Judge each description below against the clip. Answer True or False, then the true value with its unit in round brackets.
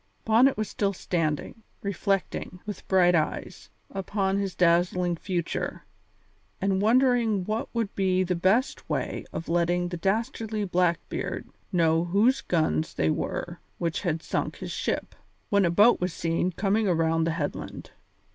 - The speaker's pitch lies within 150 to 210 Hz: True (185 Hz)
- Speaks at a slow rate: False (145 wpm)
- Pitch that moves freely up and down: False (3.3 semitones)